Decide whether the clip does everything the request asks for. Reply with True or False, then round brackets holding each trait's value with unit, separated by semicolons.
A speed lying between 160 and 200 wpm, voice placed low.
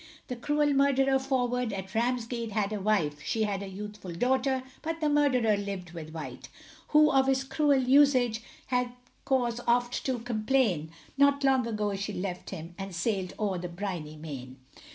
False (170 wpm; 230 Hz)